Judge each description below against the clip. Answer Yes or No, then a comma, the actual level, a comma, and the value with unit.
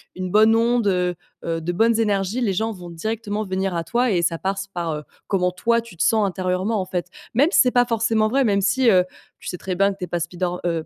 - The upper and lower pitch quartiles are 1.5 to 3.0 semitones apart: No, average, 4.0 semitones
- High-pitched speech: Yes, high, 195 Hz